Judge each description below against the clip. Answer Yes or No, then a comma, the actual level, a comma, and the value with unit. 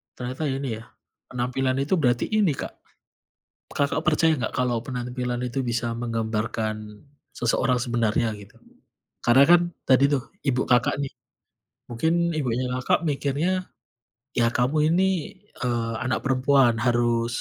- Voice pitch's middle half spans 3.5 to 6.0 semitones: No, average, 3.1 semitones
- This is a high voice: No, low, 125 Hz